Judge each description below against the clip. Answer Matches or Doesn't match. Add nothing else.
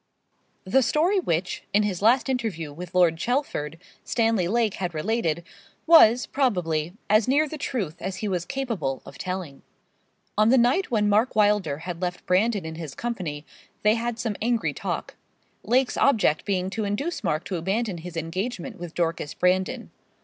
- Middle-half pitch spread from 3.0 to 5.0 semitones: Doesn't match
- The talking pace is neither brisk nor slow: Matches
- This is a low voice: Doesn't match